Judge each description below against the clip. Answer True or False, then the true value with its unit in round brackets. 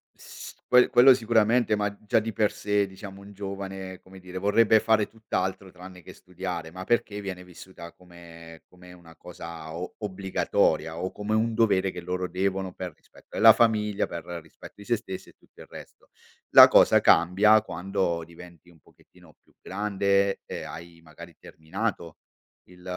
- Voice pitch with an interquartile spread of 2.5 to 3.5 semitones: True (2.8 semitones)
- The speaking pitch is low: True (95 Hz)